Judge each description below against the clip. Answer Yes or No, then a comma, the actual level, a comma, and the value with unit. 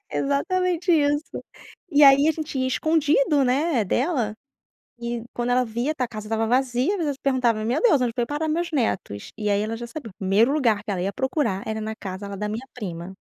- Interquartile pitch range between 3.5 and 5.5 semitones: Yes, average, 5.2 semitones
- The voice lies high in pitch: Yes, very high, 250 Hz